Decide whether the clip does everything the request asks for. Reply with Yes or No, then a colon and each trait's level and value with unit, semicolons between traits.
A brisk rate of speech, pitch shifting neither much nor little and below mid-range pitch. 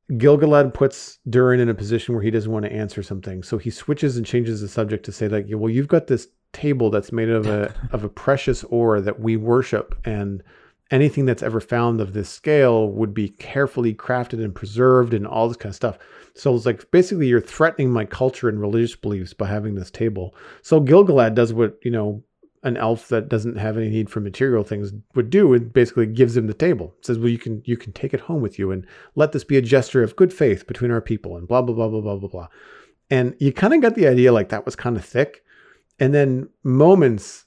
Yes: fast, 235 wpm; average, 3.4 semitones; low, 115 Hz